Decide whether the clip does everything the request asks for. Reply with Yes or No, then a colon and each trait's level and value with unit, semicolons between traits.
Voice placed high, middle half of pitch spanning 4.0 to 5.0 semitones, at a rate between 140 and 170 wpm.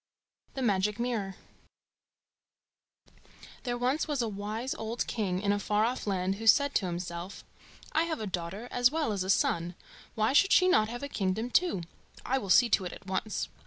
No: high, 215 Hz; average, 4.4 semitones; average, 195 wpm